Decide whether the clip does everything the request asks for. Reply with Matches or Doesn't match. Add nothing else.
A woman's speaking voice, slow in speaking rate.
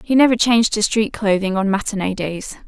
Doesn't match